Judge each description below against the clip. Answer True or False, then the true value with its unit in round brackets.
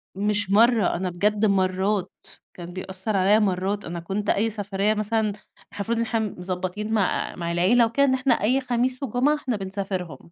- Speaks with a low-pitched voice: False (205 Hz)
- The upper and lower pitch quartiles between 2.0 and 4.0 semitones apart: True (3.2 semitones)